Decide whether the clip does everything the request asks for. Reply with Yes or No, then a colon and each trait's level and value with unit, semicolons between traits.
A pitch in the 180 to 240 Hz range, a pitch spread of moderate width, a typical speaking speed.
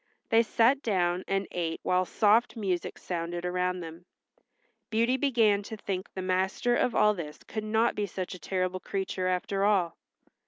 Yes: high, 190 Hz; average, 3.2 semitones; average, 165 wpm